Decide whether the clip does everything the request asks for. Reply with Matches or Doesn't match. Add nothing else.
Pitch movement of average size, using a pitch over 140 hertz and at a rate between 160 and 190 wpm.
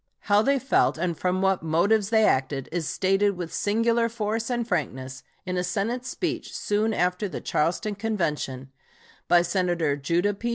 Matches